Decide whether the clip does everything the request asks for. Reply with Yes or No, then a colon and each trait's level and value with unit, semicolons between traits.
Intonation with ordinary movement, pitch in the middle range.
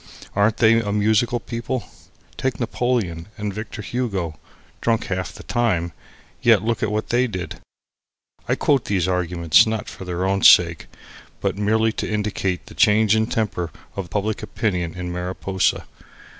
No: average, 3.7 semitones; low, 105 Hz